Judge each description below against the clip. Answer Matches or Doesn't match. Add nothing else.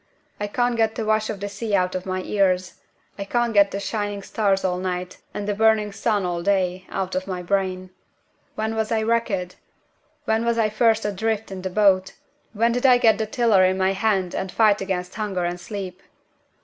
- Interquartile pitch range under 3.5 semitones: Matches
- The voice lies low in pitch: Doesn't match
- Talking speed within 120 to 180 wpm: Doesn't match